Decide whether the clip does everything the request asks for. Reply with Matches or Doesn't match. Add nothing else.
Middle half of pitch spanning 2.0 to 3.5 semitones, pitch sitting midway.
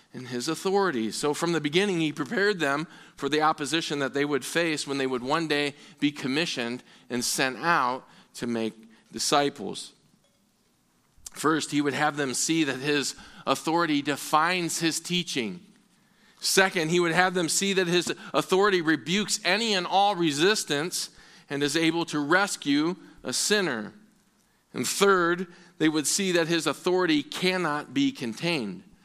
Doesn't match